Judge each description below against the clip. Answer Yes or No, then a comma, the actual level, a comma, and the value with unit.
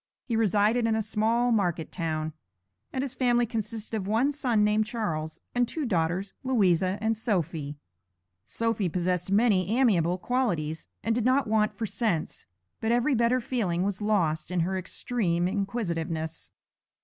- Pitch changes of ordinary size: Yes, average, 5.0 semitones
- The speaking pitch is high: Yes, high, 210 Hz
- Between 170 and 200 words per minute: No, average, 150 wpm